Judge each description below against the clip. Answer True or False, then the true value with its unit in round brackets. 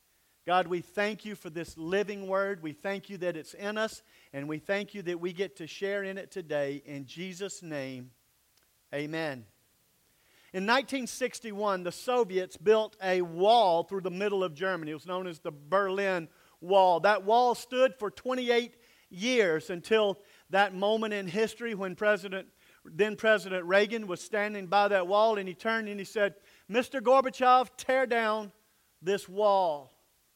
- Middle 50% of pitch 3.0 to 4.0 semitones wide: True (3.3 semitones)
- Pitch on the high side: True (195 Hz)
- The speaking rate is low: False (165 wpm)